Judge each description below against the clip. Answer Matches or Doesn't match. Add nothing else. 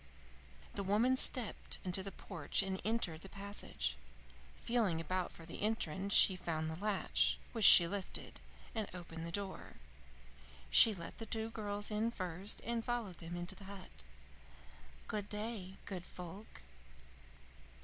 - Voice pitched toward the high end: Matches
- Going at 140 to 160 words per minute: Matches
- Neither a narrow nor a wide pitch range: Matches